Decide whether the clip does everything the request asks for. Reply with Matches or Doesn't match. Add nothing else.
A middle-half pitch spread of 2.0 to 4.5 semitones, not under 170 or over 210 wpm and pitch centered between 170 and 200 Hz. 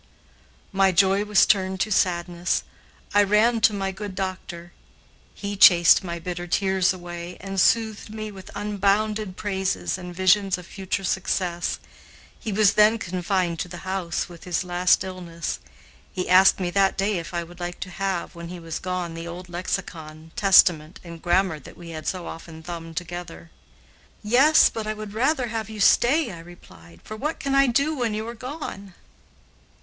Matches